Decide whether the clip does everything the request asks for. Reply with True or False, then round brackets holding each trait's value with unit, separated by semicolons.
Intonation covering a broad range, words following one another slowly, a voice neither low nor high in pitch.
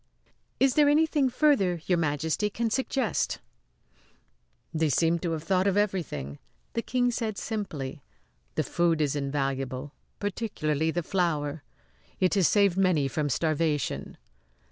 True (6.0 semitones; 130 wpm; 170 Hz)